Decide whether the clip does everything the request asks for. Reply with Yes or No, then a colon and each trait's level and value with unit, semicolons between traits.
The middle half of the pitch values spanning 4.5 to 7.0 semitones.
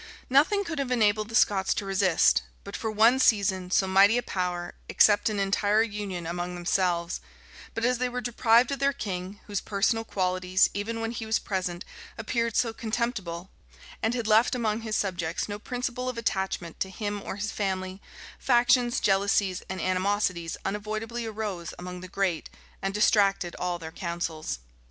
No: average, 3.5 semitones